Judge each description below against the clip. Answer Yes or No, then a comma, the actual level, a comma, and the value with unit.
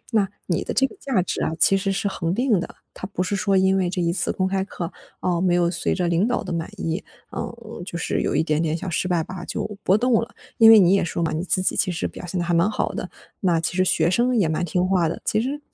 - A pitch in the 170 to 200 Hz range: Yes, medium, 185 Hz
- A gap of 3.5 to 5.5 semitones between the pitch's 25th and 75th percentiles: No, average, 2.9 semitones